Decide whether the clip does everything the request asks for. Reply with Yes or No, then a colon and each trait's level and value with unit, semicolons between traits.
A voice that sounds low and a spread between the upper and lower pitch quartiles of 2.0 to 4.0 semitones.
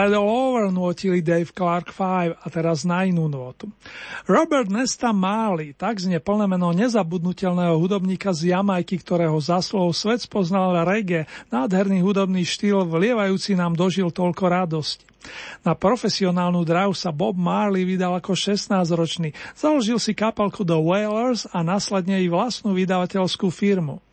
No: medium, 185 Hz; narrow, 2.6 semitones